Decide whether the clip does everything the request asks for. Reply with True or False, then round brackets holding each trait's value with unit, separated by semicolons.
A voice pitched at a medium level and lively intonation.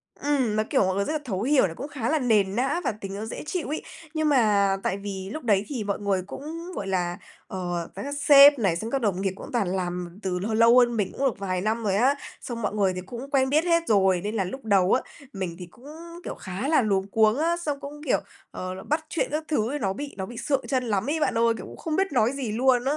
False (225 Hz; 6.2 semitones)